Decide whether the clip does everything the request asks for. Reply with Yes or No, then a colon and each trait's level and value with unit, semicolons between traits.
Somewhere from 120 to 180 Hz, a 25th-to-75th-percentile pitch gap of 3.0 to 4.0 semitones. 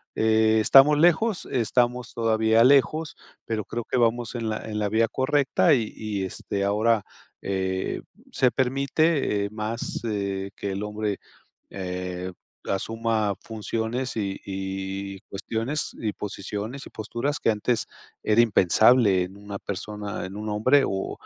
No: low, 110 Hz; average, 3.3 semitones